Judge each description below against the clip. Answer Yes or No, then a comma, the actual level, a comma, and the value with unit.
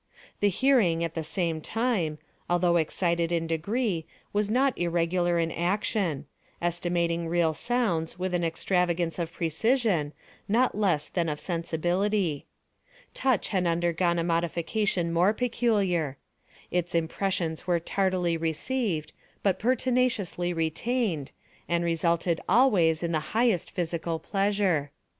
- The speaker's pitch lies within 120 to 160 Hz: No, medium, 175 Hz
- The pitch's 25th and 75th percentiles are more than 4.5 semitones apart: No, average, 3.5 semitones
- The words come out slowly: Yes, slow, 120 wpm